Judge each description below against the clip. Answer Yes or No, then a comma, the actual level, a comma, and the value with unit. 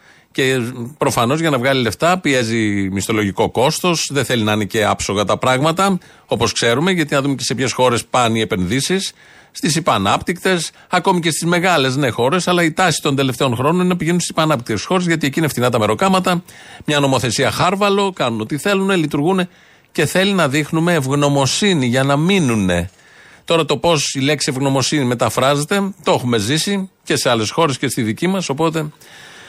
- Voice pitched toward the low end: No, medium, 145 Hz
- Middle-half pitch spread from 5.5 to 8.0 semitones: Yes, wide, 5.9 semitones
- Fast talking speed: Yes, fast, 180 wpm